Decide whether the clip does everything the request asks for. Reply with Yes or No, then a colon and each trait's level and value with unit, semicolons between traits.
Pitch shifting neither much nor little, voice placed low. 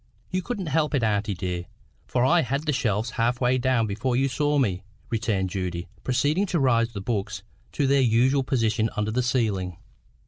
Yes: average, 4.6 semitones; low, 120 Hz